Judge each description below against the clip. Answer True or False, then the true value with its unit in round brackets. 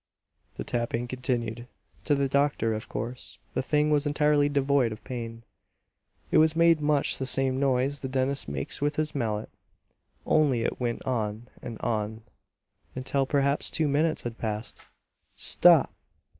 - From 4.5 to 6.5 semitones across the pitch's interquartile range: False (3.8 semitones)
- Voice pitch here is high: False (130 Hz)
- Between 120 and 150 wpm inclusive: True (145 wpm)